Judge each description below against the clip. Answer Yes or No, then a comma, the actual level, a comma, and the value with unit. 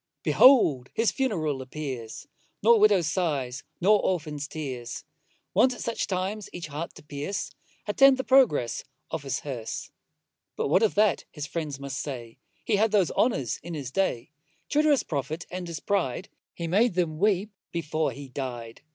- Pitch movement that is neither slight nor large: No, wide, 6.8 semitones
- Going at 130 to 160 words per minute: No, average, 170 wpm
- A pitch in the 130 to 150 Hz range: No, medium, 160 Hz